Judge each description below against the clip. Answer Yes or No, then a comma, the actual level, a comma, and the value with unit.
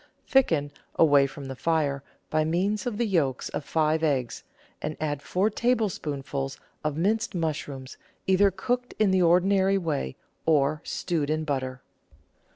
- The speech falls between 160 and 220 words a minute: No, average, 150 wpm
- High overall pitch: No, medium, 160 Hz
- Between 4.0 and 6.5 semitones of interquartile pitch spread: Yes, average, 5.2 semitones